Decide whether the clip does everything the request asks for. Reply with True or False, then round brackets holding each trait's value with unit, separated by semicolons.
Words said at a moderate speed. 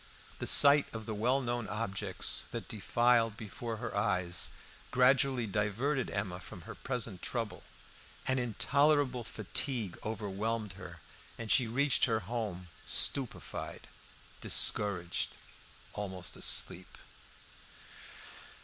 False (105 wpm)